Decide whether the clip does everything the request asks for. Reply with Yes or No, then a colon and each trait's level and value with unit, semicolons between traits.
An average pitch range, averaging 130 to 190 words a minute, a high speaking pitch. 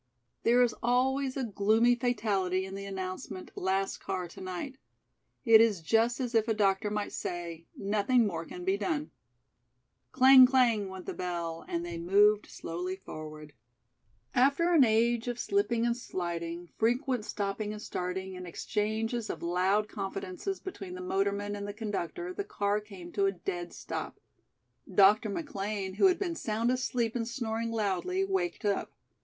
Yes: average, 4.3 semitones; average, 160 wpm; high, 210 Hz